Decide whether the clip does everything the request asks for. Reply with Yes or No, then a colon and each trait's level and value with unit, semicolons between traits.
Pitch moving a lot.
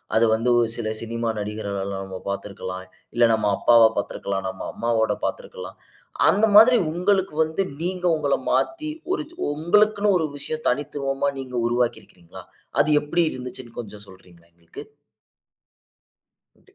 Yes: wide, 7.8 semitones